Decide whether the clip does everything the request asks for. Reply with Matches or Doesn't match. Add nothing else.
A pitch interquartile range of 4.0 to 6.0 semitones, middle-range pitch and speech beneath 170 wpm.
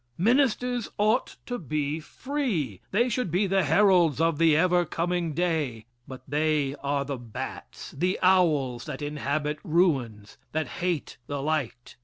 Matches